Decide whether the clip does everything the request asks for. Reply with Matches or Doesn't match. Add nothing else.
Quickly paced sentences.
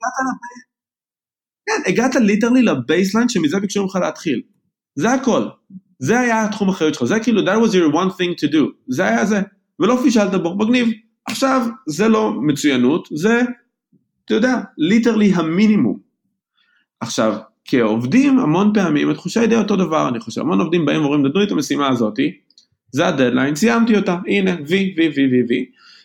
Matches